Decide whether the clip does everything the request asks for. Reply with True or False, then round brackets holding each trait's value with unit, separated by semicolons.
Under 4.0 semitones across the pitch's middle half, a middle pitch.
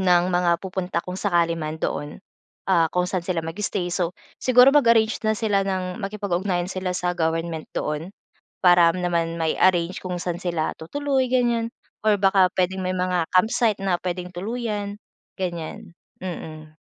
True (2.8 semitones; 180 Hz)